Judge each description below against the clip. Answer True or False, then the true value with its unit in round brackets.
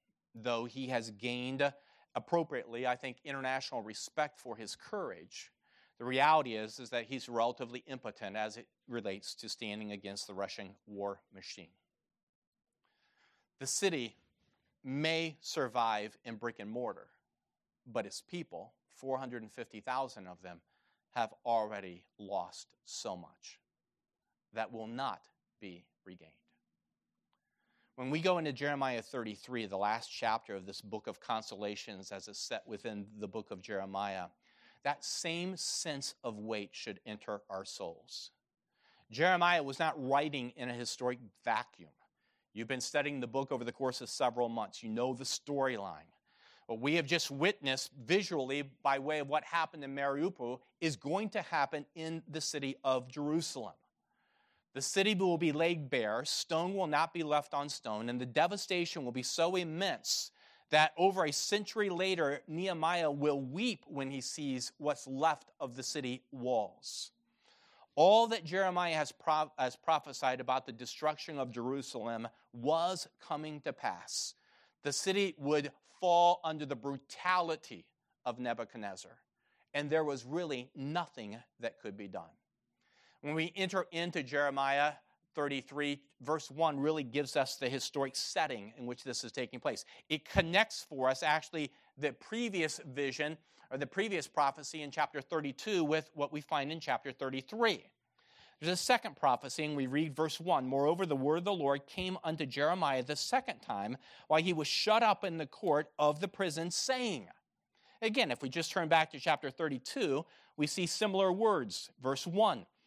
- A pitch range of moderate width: True (4.6 semitones)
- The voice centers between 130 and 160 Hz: True (140 Hz)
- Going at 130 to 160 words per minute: True (155 wpm)